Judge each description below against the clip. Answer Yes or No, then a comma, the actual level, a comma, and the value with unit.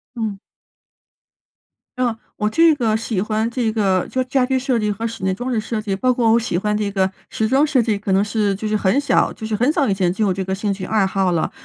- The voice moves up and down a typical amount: Yes, average, 3.5 semitones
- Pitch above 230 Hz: No, high, 215 Hz